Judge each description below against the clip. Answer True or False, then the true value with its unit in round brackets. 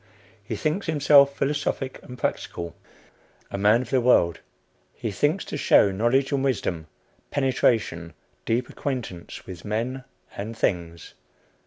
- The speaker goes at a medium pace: False (130 wpm)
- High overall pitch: False (120 Hz)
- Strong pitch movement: True (6.1 semitones)